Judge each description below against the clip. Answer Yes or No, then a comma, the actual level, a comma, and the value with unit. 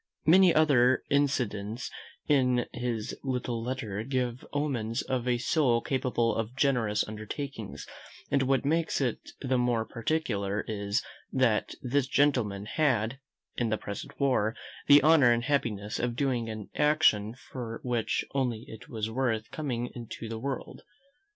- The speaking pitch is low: Yes, low, 125 Hz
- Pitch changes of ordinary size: Yes, average, 3.5 semitones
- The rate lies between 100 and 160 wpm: Yes, average, 140 wpm